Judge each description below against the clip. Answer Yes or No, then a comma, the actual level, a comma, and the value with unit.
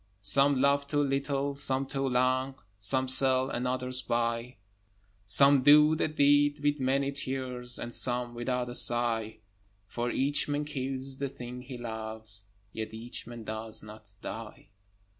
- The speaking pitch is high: No, low, 130 Hz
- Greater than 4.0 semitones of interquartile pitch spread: No, average, 2.7 semitones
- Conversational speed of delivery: Yes, average, 150 wpm